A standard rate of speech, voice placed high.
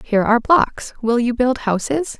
Yes: average, 190 wpm; high, 245 Hz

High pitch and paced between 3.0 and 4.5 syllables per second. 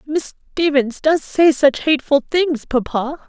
Yes: very high, 285 Hz; 4.2 syllables/s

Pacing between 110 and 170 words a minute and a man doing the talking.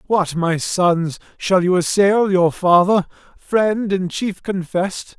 Yes: average, 140 wpm; male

